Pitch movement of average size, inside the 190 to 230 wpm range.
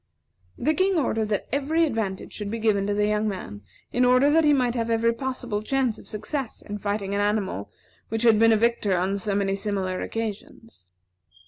Yes: average, 3.4 semitones; average, 200 wpm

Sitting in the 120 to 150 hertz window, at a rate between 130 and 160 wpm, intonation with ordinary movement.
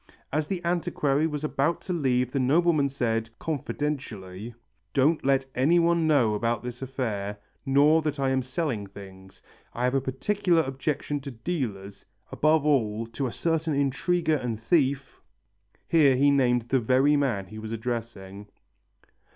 Yes: low, 135 Hz; average, 150 wpm; average, 4.7 semitones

